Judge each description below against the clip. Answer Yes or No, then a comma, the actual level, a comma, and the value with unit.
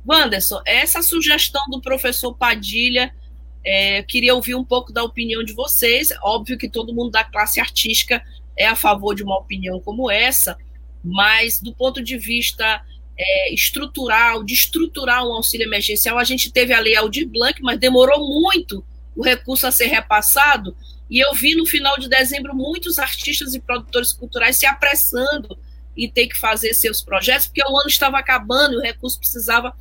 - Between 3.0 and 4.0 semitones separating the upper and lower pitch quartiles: Yes, average, 3.6 semitones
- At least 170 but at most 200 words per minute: Yes, average, 175 wpm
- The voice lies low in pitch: No, high, 245 Hz